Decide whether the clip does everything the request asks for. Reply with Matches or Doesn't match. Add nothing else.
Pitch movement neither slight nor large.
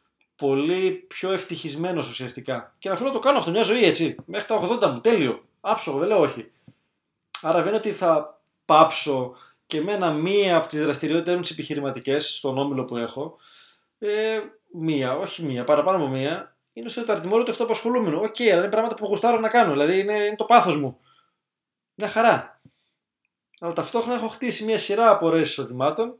Doesn't match